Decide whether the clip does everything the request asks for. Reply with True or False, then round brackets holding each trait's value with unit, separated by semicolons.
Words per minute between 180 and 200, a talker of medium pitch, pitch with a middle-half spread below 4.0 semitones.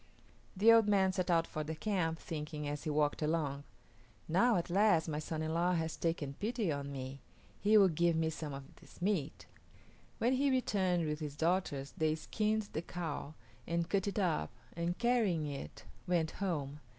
False (185 wpm; 165 Hz; 4.3 semitones)